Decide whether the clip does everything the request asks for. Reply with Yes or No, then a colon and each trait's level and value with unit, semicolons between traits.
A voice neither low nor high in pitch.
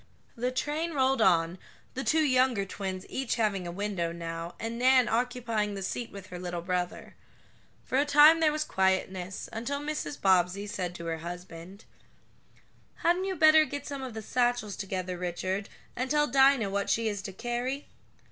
No: high, 220 Hz